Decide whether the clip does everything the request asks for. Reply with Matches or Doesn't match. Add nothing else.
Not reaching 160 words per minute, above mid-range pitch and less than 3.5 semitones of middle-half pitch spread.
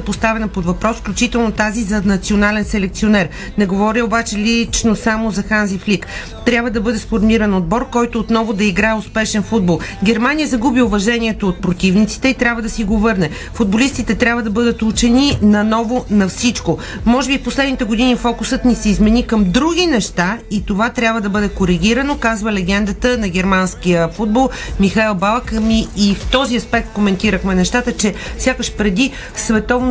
Doesn't match